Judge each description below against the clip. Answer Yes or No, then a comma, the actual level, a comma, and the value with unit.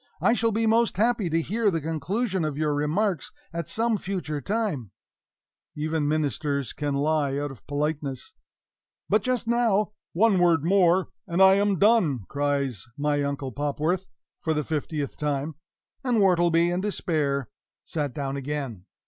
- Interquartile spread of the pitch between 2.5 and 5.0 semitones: No, wide, 5.4 semitones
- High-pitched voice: No, medium, 160 Hz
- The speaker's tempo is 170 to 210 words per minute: No, average, 155 wpm